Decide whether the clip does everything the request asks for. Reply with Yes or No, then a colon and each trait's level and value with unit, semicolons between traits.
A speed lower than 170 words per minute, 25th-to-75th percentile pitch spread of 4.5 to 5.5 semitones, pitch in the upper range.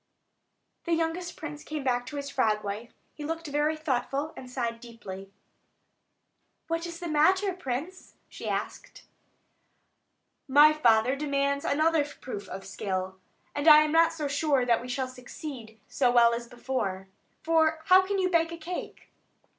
Yes: average, 155 wpm; average, 5.0 semitones; very high, 285 Hz